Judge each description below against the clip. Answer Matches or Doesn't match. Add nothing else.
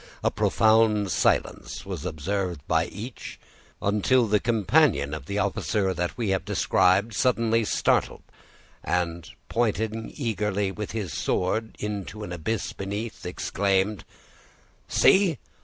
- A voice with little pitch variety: Doesn't match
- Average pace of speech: Doesn't match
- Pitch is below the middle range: Matches